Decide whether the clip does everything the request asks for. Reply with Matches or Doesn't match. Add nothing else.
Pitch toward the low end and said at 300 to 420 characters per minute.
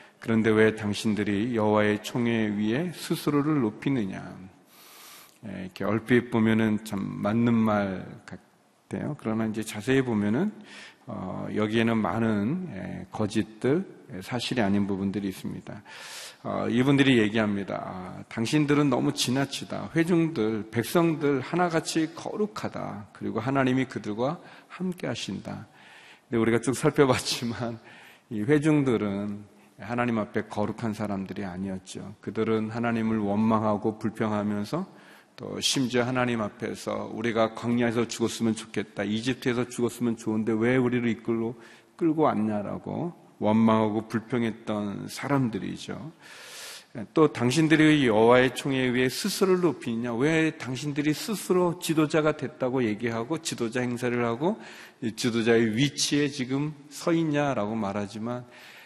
Matches